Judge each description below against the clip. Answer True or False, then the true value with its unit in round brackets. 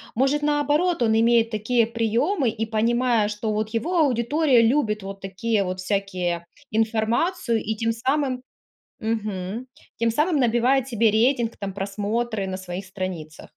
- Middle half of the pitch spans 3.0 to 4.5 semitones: True (3.4 semitones)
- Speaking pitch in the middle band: False (225 Hz)